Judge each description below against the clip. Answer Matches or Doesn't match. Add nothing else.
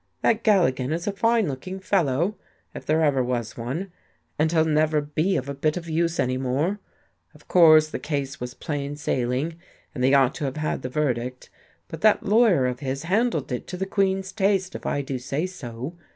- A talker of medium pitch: Matches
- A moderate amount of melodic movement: Doesn't match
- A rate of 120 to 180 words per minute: Doesn't match